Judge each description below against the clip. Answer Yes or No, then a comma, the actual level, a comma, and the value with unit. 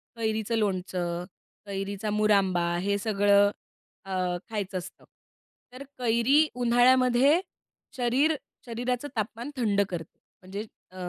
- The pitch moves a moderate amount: Yes, average, 3.7 semitones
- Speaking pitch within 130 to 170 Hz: No, high, 215 Hz